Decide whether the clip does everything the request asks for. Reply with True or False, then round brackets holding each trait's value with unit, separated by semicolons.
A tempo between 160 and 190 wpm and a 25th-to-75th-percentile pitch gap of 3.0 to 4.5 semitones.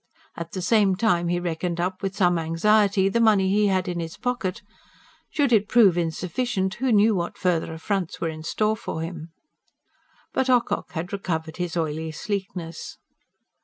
True (165 wpm; 3.9 semitones)